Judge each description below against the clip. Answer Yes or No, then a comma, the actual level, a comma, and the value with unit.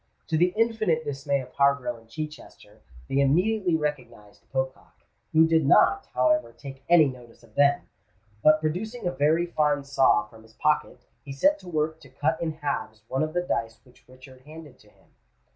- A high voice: No, medium, 145 Hz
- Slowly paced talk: No, average, 180 wpm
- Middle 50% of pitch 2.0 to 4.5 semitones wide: Yes, average, 3.6 semitones